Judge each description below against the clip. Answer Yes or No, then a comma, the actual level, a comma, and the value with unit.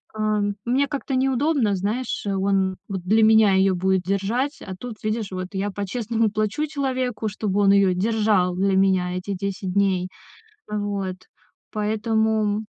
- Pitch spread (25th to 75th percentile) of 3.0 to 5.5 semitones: No, narrow, 2.6 semitones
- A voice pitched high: Yes, high, 205 Hz